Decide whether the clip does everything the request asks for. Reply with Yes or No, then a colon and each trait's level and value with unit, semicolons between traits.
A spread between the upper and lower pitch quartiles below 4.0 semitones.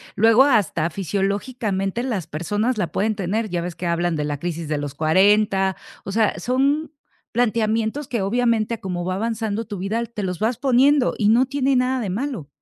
No: average, 4.6 semitones